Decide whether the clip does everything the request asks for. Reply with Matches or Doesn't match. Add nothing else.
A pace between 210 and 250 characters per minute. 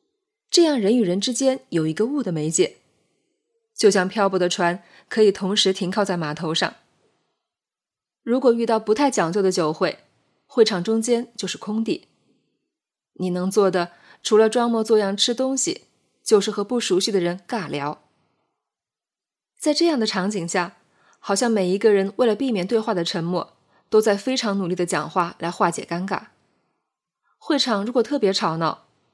Matches